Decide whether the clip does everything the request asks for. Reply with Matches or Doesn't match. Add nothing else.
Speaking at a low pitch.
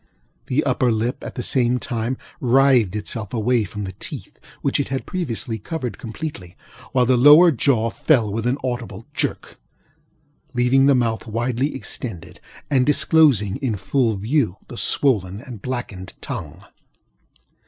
Matches